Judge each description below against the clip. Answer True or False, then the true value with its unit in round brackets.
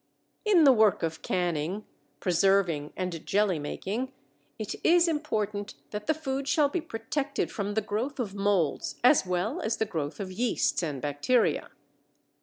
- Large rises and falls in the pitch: True (6.3 semitones)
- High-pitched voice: True (205 Hz)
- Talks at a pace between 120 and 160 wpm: True (155 wpm)